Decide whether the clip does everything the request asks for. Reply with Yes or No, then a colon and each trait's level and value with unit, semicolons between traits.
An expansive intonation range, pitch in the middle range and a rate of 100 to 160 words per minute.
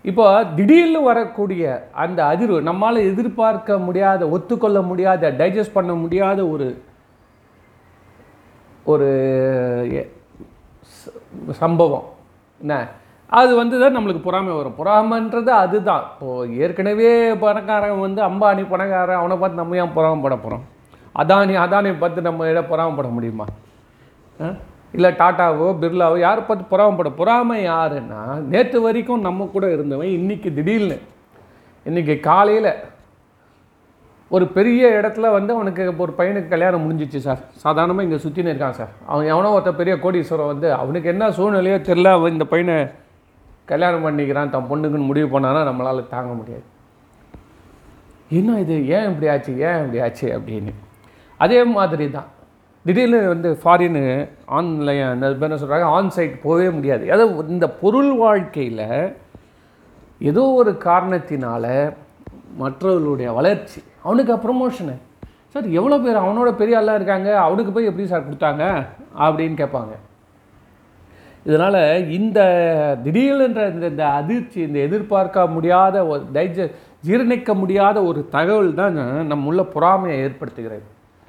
Yes: wide, 5.9 semitones; medium, 175 Hz; average, 120 wpm